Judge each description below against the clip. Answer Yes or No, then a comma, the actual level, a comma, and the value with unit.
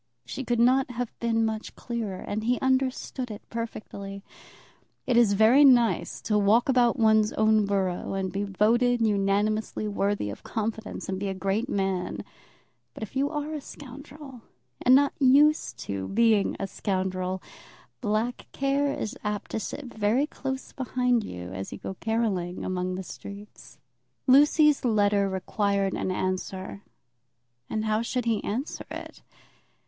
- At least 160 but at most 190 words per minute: No, average, 150 wpm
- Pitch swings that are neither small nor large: Yes, average, 4.1 semitones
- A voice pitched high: Yes, high, 220 Hz